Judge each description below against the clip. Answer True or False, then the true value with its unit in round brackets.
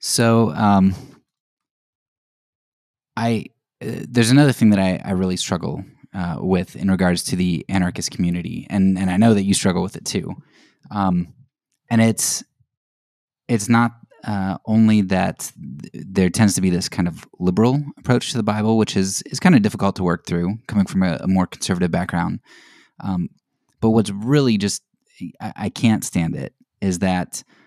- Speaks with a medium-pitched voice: False (100 Hz)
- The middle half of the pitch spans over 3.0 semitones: True (3.6 semitones)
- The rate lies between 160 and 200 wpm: True (170 wpm)